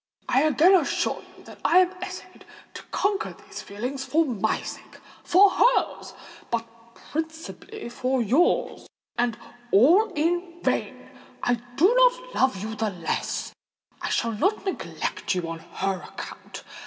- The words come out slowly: Yes, slow, 130 wpm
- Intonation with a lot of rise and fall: Yes, wide, 8.3 semitones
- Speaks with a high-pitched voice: Yes, very high, 280 Hz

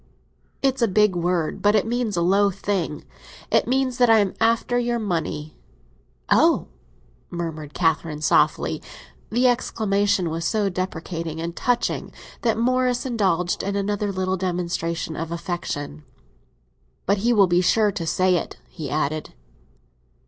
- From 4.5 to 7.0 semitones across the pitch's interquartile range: Yes, average, 4.8 semitones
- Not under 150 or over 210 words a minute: No, average, 140 wpm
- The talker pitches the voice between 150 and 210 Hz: Yes, high, 190 Hz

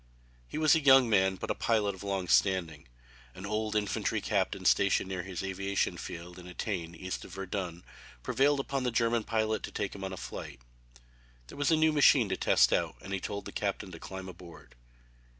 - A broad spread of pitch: No, average, 3.3 semitones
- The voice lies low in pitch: Yes, very low, 95 Hz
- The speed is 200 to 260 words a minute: Yes, fast, 205 wpm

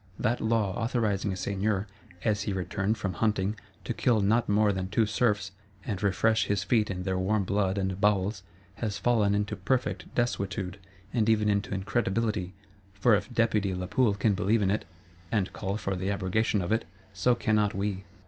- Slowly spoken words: No, average, 175 wpm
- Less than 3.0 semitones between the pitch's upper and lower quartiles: Yes, narrow, 2.4 semitones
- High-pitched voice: No, low, 100 Hz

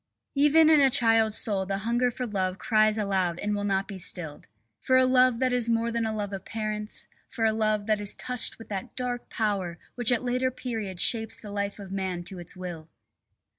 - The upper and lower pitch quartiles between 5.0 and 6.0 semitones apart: No, average, 3.7 semitones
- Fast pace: Yes, fast, 220 wpm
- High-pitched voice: Yes, high, 215 Hz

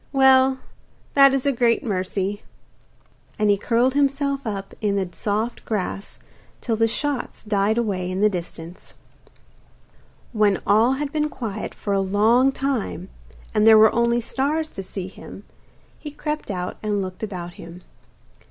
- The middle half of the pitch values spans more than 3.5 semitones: Yes, average, 5.1 semitones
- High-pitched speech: Yes, high, 220 Hz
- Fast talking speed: No, average, 150 wpm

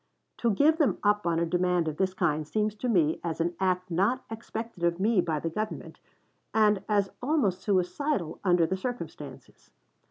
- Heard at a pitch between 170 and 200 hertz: Yes, high, 190 Hz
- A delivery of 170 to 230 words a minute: Yes, average, 180 wpm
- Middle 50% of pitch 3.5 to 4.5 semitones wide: Yes, average, 4.1 semitones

